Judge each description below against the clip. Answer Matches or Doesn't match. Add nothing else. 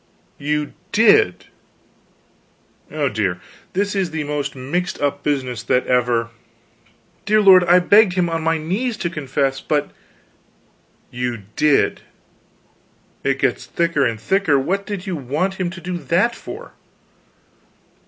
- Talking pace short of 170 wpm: Matches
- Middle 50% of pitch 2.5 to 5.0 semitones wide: Doesn't match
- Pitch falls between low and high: Matches